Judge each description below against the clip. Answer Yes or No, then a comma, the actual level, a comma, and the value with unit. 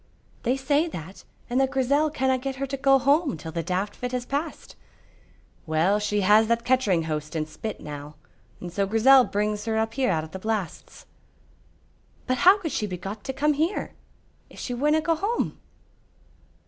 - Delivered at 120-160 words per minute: No, average, 185 wpm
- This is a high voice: Yes, high, 240 Hz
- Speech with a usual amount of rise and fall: No, wide, 6.1 semitones